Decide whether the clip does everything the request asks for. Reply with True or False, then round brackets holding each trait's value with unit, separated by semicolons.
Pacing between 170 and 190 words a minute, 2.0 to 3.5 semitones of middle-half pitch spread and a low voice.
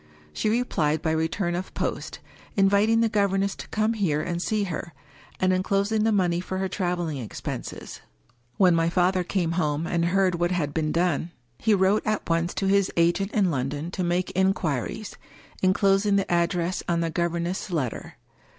False (175 wpm; 2.7 semitones; 180 Hz)